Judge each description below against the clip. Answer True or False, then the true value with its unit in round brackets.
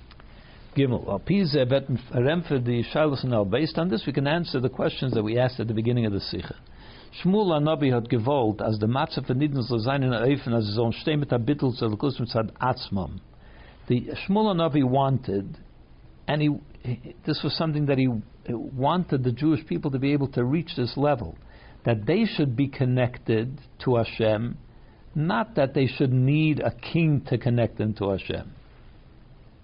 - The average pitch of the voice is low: True (130 Hz)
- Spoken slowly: True (130 wpm)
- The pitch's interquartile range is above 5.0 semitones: False (4.3 semitones)